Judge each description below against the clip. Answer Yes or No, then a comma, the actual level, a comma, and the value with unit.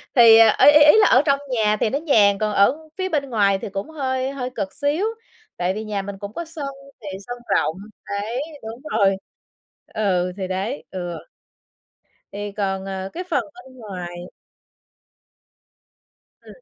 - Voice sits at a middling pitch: No, high, 220 Hz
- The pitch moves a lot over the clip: Yes, wide, 5.9 semitones